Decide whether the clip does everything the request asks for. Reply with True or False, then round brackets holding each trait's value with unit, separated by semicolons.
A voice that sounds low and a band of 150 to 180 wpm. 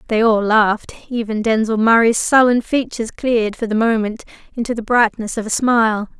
False (225 Hz; 165 wpm)